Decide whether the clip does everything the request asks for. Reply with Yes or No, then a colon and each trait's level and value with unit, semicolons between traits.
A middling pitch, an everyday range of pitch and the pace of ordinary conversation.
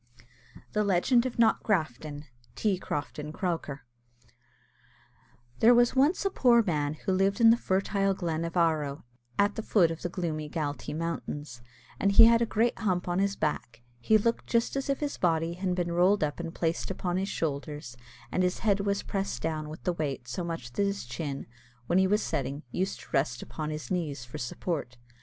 Yes: medium, 175 Hz; average, 4.8 semitones; average, 190 wpm